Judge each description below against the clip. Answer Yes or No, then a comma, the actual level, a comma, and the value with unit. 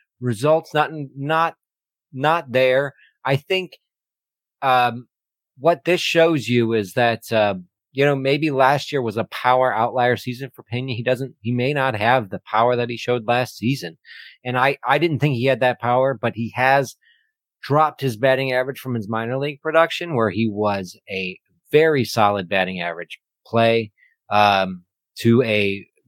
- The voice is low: Yes, low, 125 Hz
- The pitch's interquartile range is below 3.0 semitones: No, average, 3.7 semitones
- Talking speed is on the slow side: No, average, 170 wpm